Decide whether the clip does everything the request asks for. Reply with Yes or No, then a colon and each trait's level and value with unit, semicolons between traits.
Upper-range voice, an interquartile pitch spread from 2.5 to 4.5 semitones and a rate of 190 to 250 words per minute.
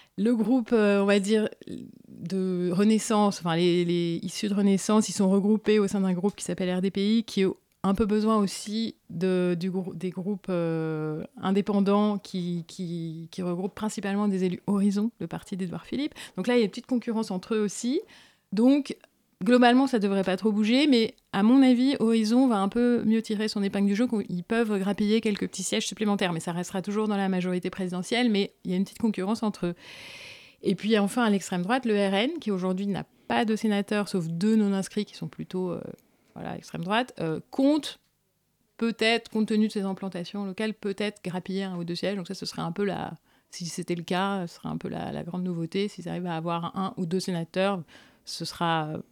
Yes: high, 200 Hz; average, 3.0 semitones; average, 215 wpm